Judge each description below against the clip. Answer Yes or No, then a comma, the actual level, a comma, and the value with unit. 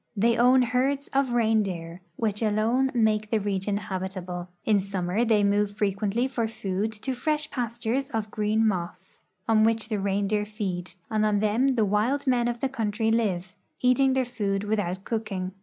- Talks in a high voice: Yes, high, 215 Hz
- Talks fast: No, average, 170 wpm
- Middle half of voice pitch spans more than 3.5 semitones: No, average, 3.1 semitones